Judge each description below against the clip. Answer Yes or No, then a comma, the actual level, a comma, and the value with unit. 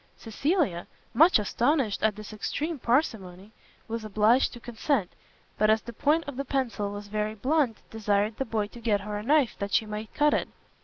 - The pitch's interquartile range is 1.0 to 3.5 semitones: No, average, 4.3 semitones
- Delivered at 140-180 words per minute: No, average, 190 wpm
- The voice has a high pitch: Yes, high, 220 Hz